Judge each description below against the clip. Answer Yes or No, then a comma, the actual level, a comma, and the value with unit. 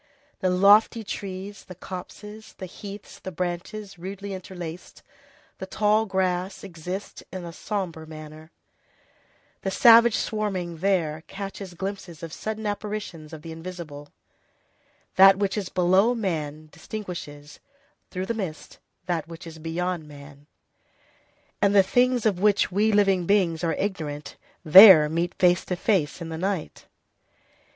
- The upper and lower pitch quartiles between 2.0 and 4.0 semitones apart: Yes, average, 3.6 semitones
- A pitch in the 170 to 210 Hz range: Yes, medium, 185 Hz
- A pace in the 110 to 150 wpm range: Yes, slow, 135 wpm